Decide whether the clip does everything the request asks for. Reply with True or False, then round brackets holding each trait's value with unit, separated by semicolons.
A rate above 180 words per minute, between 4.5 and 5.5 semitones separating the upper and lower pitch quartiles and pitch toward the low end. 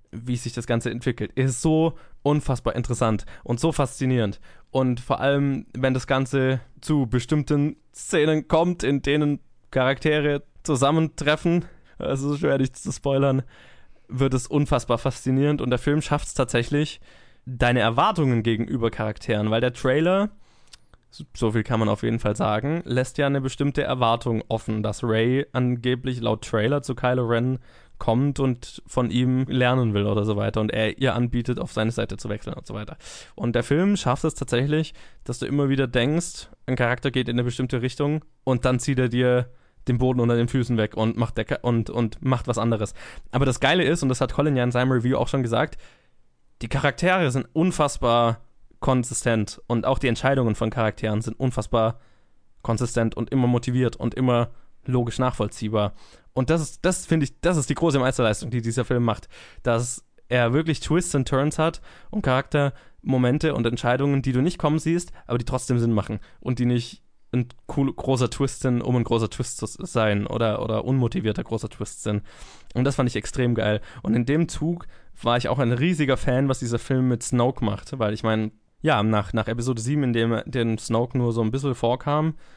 False (190 wpm; 3.2 semitones; 125 Hz)